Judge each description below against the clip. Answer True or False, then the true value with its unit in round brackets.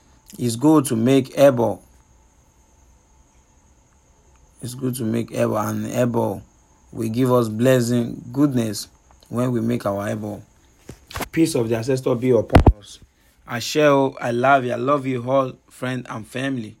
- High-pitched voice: False (115 Hz)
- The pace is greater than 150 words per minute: False (135 wpm)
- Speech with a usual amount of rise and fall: False (6.9 semitones)